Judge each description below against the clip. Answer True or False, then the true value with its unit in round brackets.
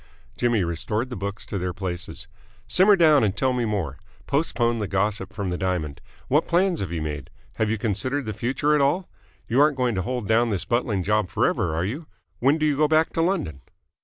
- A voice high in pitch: False (110 Hz)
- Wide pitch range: True (7.0 semitones)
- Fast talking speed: True (215 wpm)